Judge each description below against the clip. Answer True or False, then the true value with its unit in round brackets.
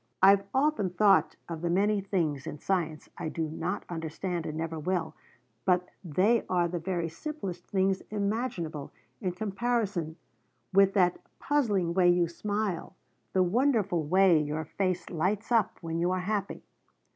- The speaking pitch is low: False (185 Hz)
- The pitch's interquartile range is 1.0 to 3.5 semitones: True (3.2 semitones)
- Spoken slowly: False (150 wpm)